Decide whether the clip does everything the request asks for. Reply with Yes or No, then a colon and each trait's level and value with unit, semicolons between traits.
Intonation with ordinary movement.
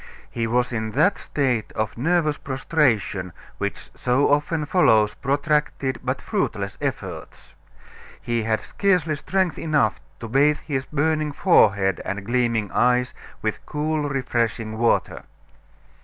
Yes: average, 4.9 semitones